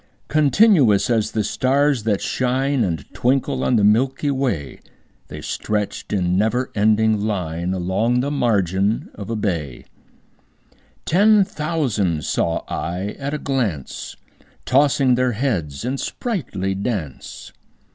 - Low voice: Yes, low, 115 Hz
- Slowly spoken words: Yes, slow, 125 wpm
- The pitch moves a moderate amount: No, wide, 5.9 semitones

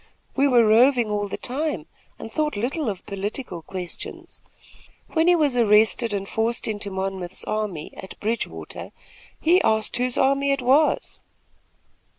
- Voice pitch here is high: Yes, high, 225 Hz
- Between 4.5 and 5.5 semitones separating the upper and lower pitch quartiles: Yes, average, 5.1 semitones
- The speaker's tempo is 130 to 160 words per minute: Yes, average, 145 wpm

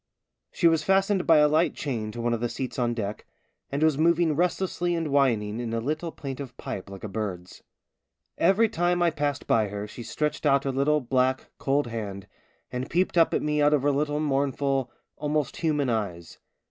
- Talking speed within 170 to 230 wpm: Yes, average, 195 wpm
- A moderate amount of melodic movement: Yes, average, 4.8 semitones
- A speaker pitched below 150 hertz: Yes, medium, 140 Hz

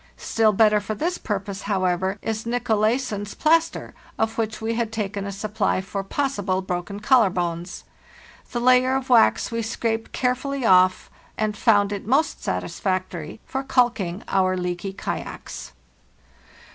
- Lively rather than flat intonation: No, average, 3.9 semitones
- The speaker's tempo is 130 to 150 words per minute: Yes, average, 145 wpm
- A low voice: No, high, 215 Hz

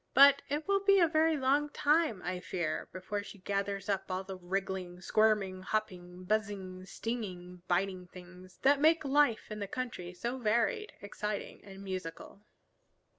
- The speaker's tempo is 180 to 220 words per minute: No, average, 155 wpm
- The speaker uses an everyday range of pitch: No, wide, 6.1 semitones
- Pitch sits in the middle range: No, high, 200 Hz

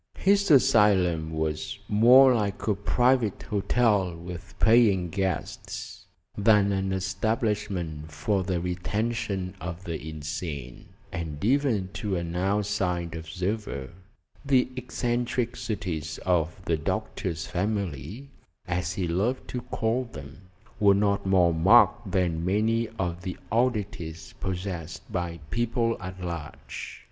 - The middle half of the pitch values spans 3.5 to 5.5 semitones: Yes, average, 4.3 semitones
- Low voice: Yes, very low, 95 Hz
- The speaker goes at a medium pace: No, slow, 115 wpm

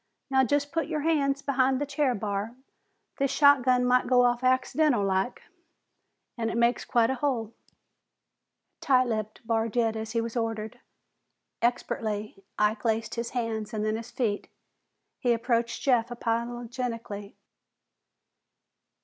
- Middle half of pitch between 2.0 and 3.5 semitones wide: Yes, narrow, 2.5 semitones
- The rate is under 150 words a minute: Yes, slow, 135 wpm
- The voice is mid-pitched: No, high, 235 Hz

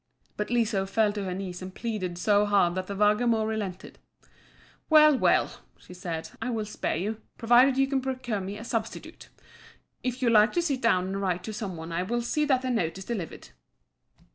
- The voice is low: No, high, 210 Hz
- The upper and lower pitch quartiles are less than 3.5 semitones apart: No, average, 4.3 semitones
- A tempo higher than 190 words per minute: Yes, average, 200 wpm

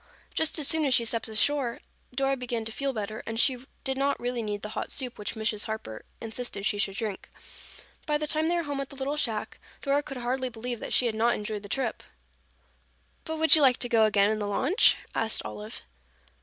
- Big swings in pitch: No, average, 4.1 semitones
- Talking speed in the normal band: No, fast, 225 wpm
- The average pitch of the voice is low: No, high, 240 Hz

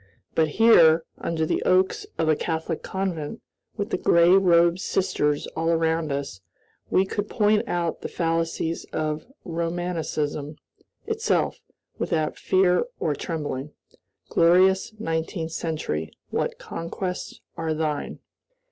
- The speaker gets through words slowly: Yes, slow, 120 wpm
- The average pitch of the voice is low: No, medium, 165 Hz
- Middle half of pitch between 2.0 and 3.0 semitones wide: Yes, narrow, 2.6 semitones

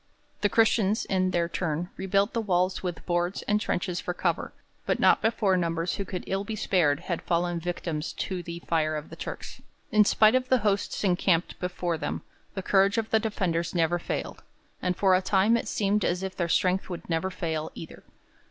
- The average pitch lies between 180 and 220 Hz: Yes, medium, 185 Hz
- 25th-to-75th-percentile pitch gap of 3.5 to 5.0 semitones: No, narrow, 2.6 semitones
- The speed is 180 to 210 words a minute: Yes, average, 200 wpm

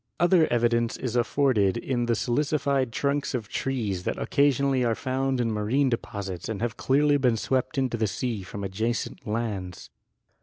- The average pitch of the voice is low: Yes, low, 120 Hz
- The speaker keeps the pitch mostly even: No, average, 3.5 semitones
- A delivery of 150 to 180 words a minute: Yes, average, 165 wpm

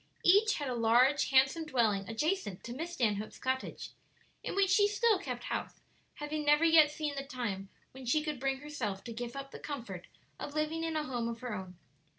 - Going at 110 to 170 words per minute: No, average, 200 wpm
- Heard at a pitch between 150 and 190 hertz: No, very high, 275 Hz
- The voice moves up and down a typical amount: Yes, average, 4.9 semitones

